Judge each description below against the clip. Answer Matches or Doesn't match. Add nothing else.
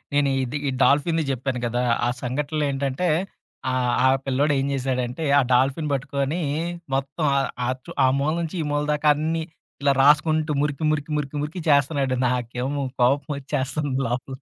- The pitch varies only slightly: Matches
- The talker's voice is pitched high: Doesn't match